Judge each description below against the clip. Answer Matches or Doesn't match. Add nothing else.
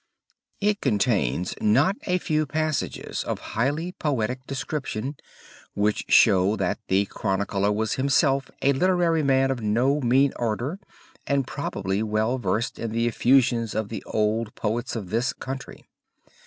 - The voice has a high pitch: Doesn't match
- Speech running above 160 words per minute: Doesn't match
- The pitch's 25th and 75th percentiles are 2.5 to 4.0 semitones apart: Doesn't match